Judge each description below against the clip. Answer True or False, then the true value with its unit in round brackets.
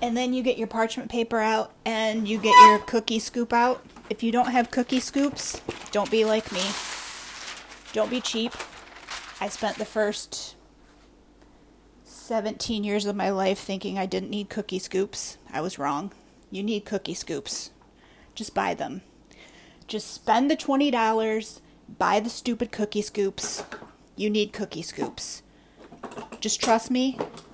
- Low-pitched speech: False (220 Hz)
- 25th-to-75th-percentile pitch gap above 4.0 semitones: False (2.5 semitones)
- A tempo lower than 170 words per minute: True (150 wpm)